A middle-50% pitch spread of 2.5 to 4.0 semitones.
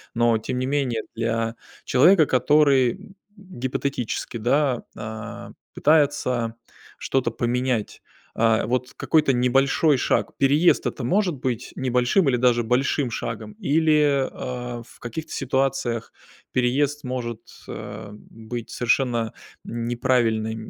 Yes: average, 3.0 semitones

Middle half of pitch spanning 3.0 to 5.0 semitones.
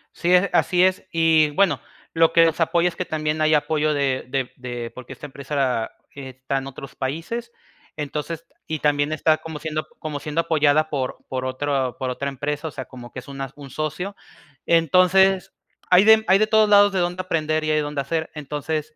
Yes: average, 3.3 semitones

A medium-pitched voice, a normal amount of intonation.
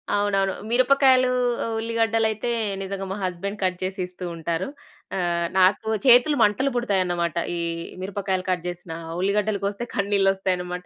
No: high, 195 Hz; average, 3.2 semitones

